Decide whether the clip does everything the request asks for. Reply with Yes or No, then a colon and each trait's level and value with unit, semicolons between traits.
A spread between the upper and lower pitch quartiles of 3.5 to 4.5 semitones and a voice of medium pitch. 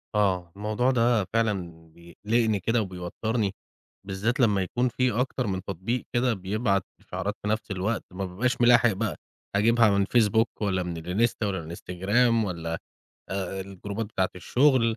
No: average, 3.8 semitones; low, 105 Hz